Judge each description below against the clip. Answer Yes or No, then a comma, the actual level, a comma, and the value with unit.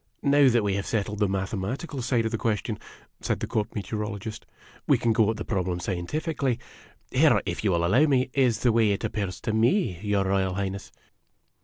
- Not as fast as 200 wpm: No, fast, 205 wpm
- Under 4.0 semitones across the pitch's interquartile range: Yes, average, 3.6 semitones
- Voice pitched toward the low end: Yes, low, 110 Hz